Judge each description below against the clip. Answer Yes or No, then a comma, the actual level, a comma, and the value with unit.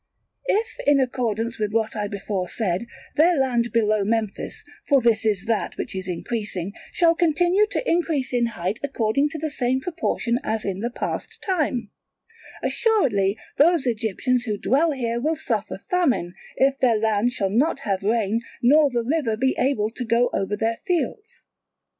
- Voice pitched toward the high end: Yes, high, 235 Hz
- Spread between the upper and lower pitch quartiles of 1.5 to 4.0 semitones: No, average, 5.0 semitones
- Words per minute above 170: No, average, 165 wpm